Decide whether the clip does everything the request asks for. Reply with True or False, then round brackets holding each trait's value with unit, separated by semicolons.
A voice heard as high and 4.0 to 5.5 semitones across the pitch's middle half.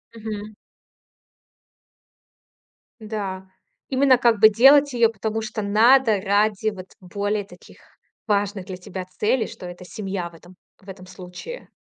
False (205 Hz; 2.9 semitones)